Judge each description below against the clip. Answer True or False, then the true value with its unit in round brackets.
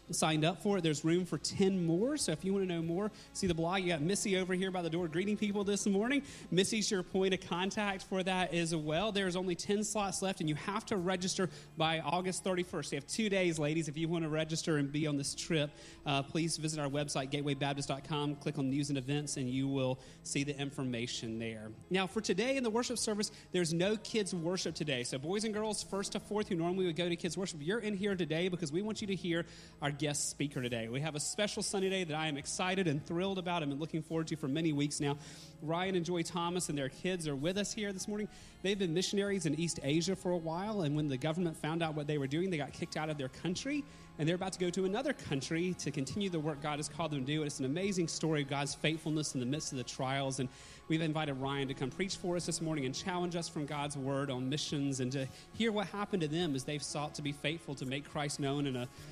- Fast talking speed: True (260 wpm)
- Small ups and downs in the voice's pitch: False (4.4 semitones)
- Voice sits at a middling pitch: True (165 Hz)